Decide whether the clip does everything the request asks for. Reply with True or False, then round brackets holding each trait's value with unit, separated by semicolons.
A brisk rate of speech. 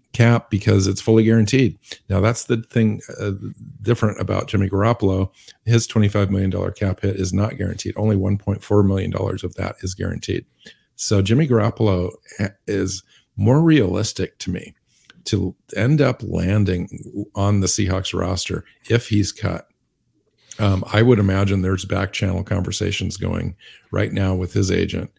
False (160 wpm)